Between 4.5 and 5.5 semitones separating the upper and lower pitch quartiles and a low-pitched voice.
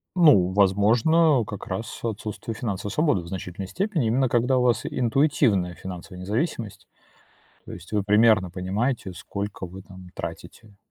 Yes: average, 4.8 semitones; low, 105 Hz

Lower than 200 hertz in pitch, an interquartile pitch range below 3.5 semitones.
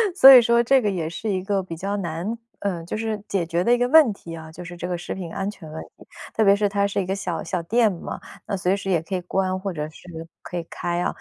Yes: high, 190 Hz; average, 3.1 semitones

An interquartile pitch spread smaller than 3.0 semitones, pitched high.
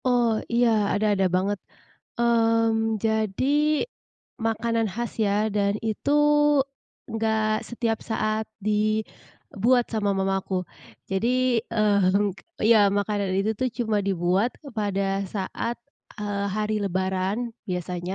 Yes: narrow, 2.4 semitones; high, 215 Hz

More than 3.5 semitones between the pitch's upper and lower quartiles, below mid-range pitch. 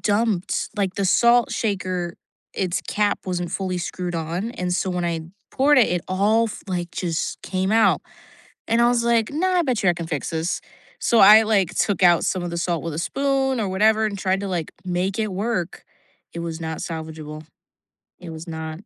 No: average, 4.2 semitones; medium, 185 Hz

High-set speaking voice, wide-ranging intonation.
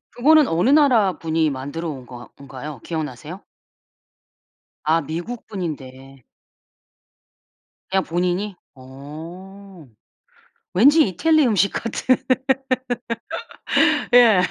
No: medium, 175 Hz; wide, 6.4 semitones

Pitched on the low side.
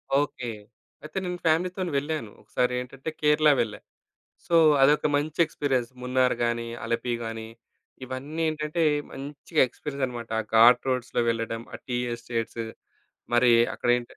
Yes: low, 130 Hz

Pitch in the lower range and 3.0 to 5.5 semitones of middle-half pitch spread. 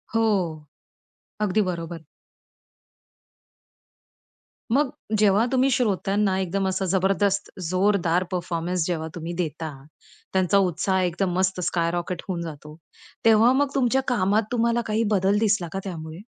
No: high, 190 Hz; average, 3.4 semitones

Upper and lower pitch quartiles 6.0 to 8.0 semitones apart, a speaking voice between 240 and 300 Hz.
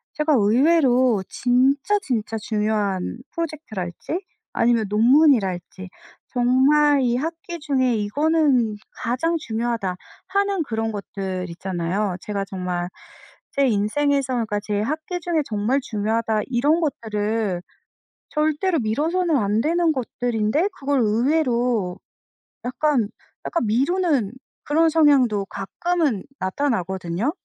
Yes: wide, 6.3 semitones; high, 245 Hz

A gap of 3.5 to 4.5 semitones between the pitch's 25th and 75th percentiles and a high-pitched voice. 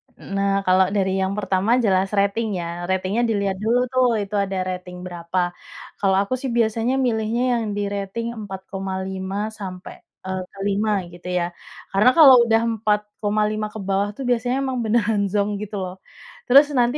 No: average, 2.8 semitones; high, 200 Hz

